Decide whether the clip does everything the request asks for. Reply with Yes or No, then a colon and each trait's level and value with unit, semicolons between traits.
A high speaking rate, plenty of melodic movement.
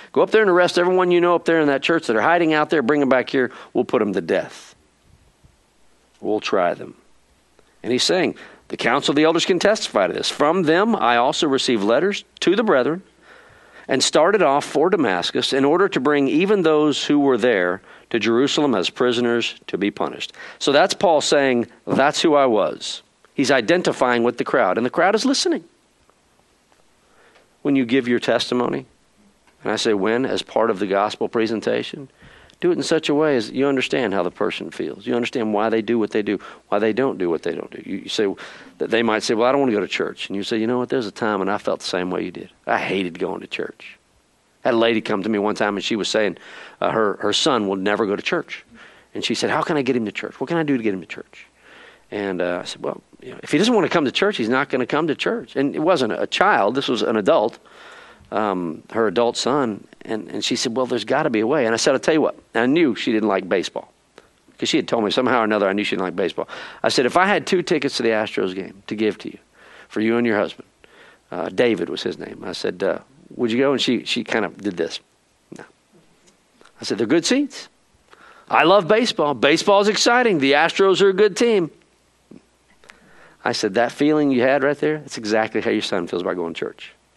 Yes: fast, 245 wpm; wide, 6.4 semitones